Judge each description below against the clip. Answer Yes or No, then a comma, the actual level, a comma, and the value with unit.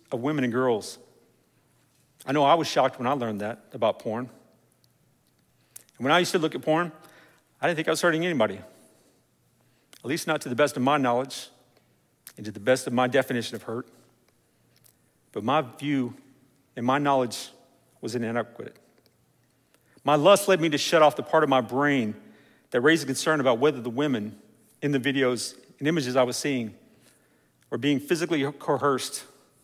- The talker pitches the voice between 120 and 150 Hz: Yes, low, 135 Hz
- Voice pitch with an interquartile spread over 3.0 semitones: Yes, average, 3.4 semitones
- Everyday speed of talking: Yes, average, 180 wpm